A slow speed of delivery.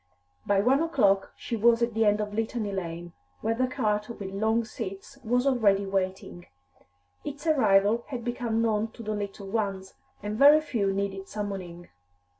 No: average, 165 wpm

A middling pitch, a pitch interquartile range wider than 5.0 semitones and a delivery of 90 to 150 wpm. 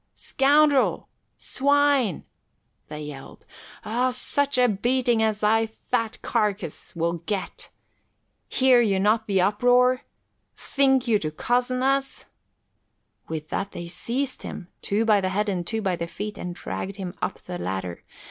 No: high, 215 Hz; wide, 5.5 semitones; average, 145 wpm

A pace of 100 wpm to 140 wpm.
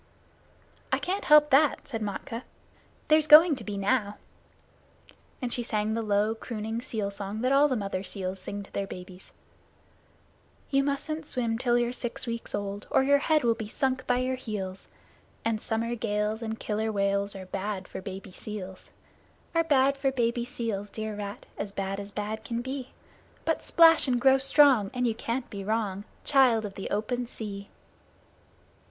No: average, 175 wpm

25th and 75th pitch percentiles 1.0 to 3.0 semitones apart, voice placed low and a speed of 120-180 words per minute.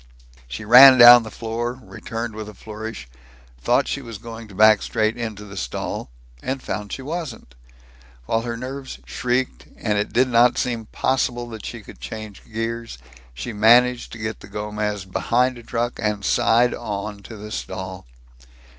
Yes: narrow, 2.4 semitones; low, 115 Hz; average, 170 wpm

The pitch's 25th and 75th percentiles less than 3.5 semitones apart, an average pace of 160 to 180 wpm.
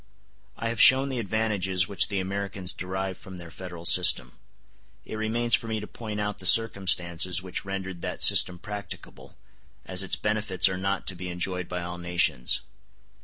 Yes: average, 2.7 semitones; average, 170 wpm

